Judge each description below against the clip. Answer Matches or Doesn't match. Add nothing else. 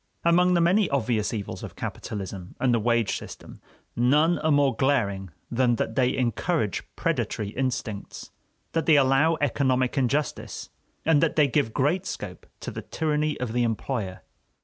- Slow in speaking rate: Doesn't match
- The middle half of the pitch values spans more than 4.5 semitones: Matches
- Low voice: Matches